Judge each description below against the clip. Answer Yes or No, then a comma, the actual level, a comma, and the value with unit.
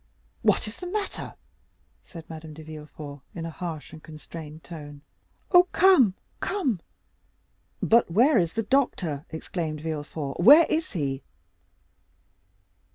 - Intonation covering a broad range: Yes, wide, 7.3 semitones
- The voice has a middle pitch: Yes, medium, 165 Hz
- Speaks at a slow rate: Yes, slow, 125 wpm